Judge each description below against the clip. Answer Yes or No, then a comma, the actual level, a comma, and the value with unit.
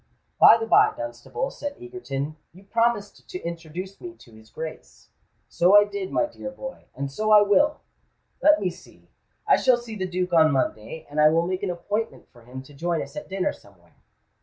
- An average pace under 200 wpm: Yes, average, 190 wpm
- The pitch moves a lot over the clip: Yes, wide, 6.6 semitones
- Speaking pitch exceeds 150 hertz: Yes, medium, 185 Hz